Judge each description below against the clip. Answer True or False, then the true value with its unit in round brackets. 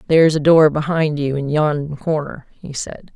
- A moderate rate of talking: True (190 wpm)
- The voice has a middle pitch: True (150 Hz)